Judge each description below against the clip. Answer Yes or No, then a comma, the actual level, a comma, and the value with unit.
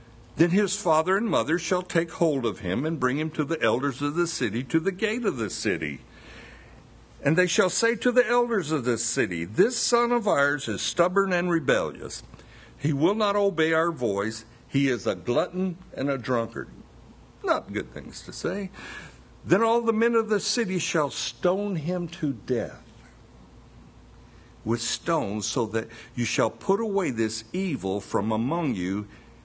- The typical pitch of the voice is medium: Yes, medium, 160 Hz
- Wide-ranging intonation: Yes, wide, 8.2 semitones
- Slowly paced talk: No, average, 175 wpm